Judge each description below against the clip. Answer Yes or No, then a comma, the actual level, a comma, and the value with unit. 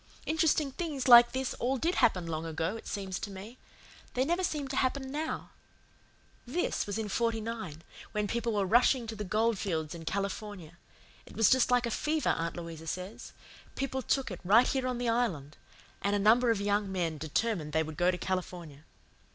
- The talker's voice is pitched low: No, high, 215 Hz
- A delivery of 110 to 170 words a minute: No, average, 190 wpm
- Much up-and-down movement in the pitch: Yes, wide, 5.9 semitones